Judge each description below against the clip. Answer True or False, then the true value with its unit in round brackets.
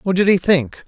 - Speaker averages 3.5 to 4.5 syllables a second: False (4.8 syllables/s)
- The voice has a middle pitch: True (175 Hz)